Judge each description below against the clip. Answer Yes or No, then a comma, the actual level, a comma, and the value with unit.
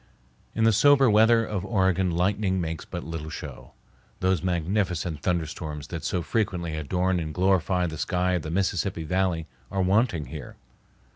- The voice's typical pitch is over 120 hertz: No, very low, 90 Hz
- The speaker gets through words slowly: No, average, 155 wpm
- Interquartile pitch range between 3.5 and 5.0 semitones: No, average, 3.0 semitones